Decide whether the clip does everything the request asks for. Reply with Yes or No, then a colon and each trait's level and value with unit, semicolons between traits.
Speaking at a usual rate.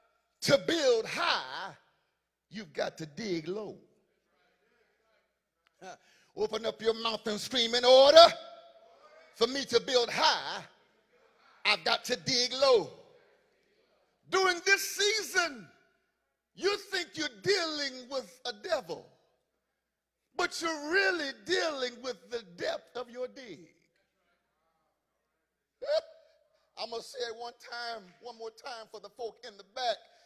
No: slow, 125 wpm